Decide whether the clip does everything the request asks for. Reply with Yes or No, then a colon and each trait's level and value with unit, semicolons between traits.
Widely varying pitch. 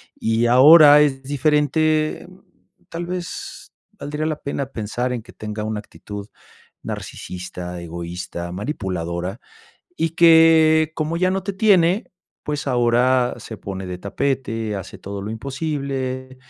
Yes: wide, 6.8 semitones